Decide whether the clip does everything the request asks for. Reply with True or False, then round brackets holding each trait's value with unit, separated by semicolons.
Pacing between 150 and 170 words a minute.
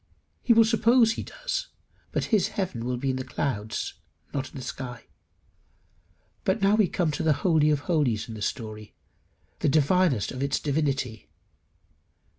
True (165 wpm)